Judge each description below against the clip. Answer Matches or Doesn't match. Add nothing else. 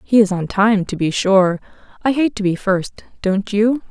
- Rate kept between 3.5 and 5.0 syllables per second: Matches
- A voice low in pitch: Doesn't match